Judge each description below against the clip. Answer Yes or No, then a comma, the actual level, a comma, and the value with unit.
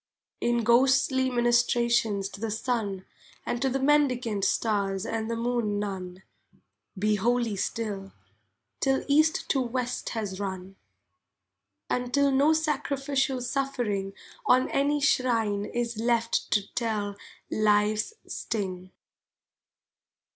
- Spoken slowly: Yes, slow, 110 wpm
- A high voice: Yes, high, 235 Hz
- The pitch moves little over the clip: No, average, 4.2 semitones